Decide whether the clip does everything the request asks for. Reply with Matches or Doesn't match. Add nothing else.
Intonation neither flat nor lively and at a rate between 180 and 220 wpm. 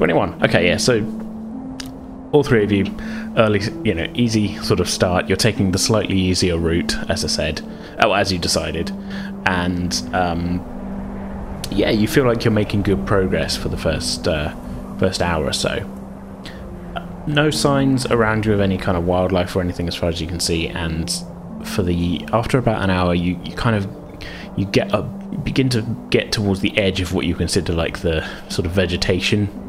Matches